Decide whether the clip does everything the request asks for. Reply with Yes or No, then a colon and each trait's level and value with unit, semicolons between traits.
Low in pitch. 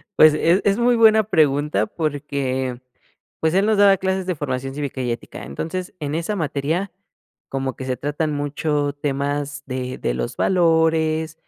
No: medium, 150 Hz